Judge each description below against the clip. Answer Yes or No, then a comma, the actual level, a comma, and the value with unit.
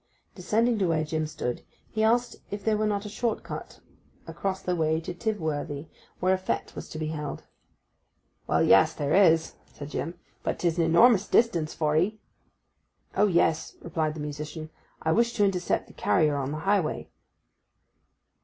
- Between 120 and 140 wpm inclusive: No, average, 170 wpm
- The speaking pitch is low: No, medium, 170 Hz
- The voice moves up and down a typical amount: Yes, average, 4.8 semitones